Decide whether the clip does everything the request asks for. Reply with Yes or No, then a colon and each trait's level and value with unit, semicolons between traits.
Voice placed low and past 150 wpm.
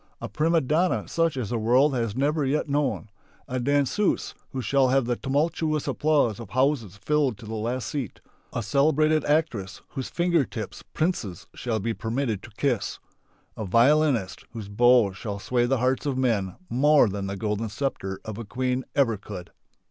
Yes: low, 125 Hz; average, 175 wpm